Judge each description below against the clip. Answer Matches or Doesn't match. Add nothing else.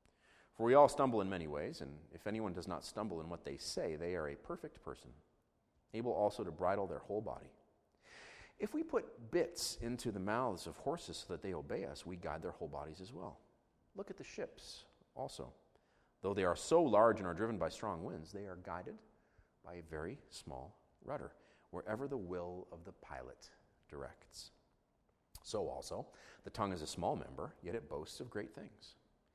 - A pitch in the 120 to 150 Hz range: Doesn't match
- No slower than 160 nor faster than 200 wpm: Matches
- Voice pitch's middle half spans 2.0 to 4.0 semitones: Doesn't match